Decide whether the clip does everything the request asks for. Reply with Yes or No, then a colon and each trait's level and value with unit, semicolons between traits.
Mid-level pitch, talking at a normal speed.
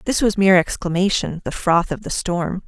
Yes: medium, 180 Hz; average, 180 wpm